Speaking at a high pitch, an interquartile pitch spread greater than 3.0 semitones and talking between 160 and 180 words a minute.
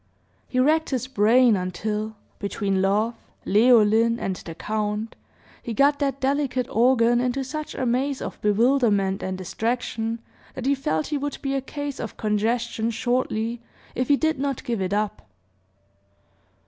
No: high, 235 Hz; average, 4.1 semitones; average, 150 wpm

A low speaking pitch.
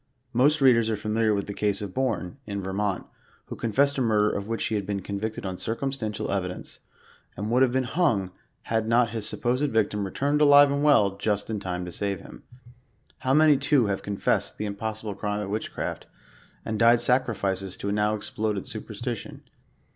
Yes: low, 110 Hz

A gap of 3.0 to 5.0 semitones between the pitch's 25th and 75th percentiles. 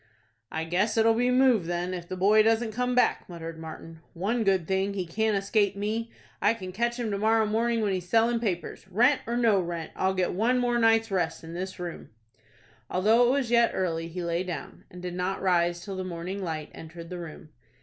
Yes: average, 4.5 semitones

